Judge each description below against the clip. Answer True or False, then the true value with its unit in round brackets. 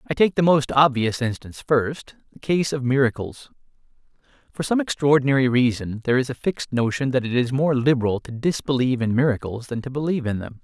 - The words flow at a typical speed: True (190 wpm)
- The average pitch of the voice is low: True (130 Hz)